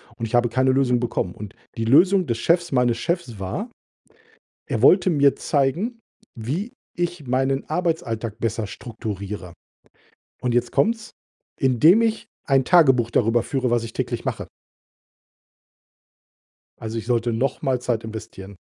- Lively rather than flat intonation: Yes, wide, 6.1 semitones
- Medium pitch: No, low, 125 Hz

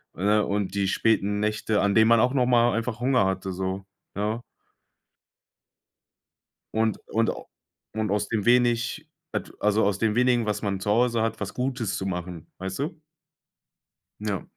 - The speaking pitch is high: No, low, 110 Hz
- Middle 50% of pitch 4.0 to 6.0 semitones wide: No, average, 2.9 semitones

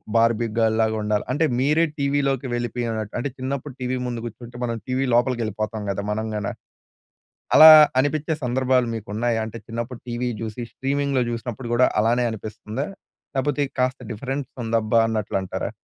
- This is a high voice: No, low, 120 Hz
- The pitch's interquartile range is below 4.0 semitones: Yes, average, 2.9 semitones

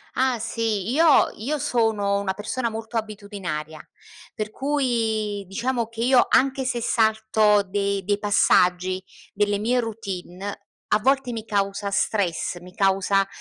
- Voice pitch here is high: Yes, high, 210 Hz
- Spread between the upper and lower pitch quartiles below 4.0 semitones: Yes, average, 2.8 semitones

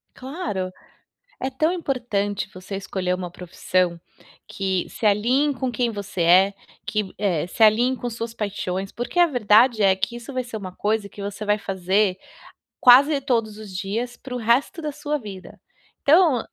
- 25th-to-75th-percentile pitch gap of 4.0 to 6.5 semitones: Yes, average, 4.5 semitones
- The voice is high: Yes, high, 215 Hz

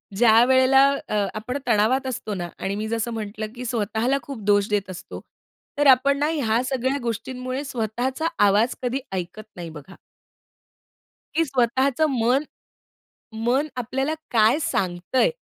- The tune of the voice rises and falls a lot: No, average, 3.6 semitones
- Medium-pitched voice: No, high, 240 Hz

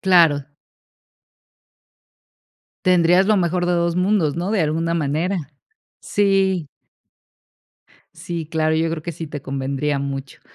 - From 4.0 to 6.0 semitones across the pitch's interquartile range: No, average, 3.3 semitones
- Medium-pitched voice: Yes, medium, 165 Hz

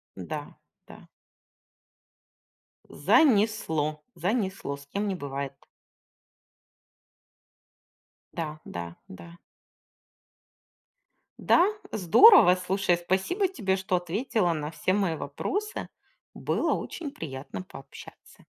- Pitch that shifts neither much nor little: No, wide, 5.7 semitones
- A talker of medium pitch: Yes, medium, 180 Hz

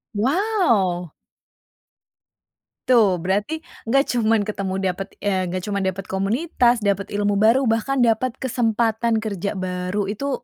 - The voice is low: No, high, 215 Hz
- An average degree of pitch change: Yes, average, 3.8 semitones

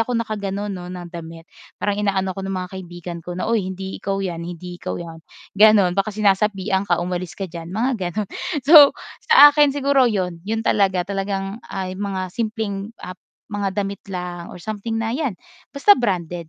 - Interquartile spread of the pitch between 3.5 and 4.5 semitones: No, average, 3.1 semitones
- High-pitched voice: Yes, high, 195 Hz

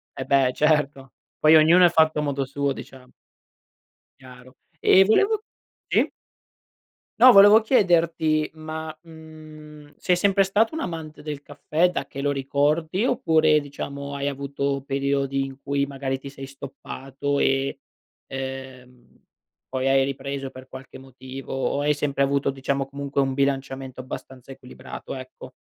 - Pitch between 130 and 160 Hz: Yes, medium, 140 Hz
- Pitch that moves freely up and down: No, narrow, 2.6 semitones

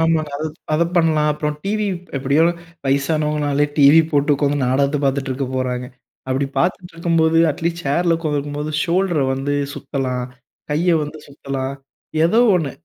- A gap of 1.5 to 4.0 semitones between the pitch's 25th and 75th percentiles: Yes, average, 2.8 semitones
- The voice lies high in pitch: No, medium, 150 Hz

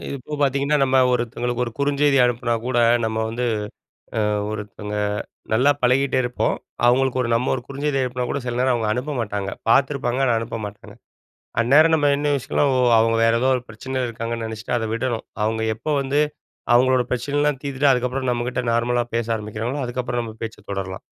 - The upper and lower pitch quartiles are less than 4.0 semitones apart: Yes, narrow, 2.6 semitones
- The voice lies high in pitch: No, low, 125 Hz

